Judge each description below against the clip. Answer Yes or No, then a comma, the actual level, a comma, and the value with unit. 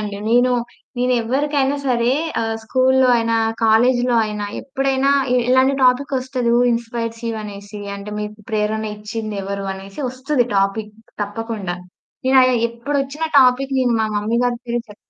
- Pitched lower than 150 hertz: No, high, 235 Hz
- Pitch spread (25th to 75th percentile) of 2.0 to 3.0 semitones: No, average, 3.5 semitones